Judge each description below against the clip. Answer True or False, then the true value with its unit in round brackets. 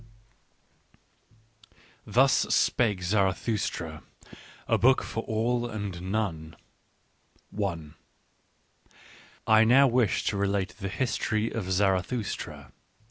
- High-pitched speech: False (105 Hz)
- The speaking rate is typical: False (90 wpm)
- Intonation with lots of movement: False (3.6 semitones)